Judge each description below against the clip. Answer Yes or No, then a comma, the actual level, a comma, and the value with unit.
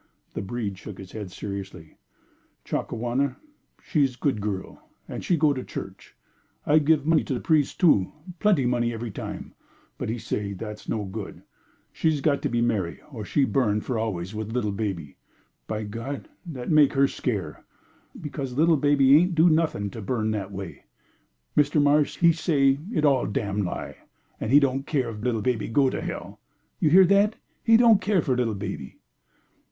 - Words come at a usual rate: Yes, average, 180 wpm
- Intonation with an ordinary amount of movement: No, wide, 5.9 semitones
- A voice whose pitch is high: No, low, 125 Hz